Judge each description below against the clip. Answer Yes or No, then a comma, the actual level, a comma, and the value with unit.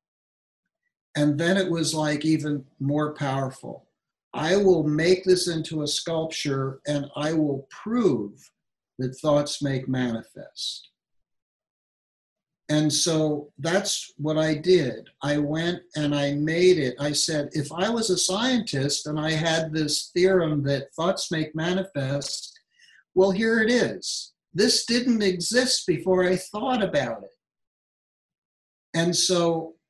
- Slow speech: Yes, slow, 130 wpm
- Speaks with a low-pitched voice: No, medium, 155 Hz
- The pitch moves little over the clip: No, average, 4.1 semitones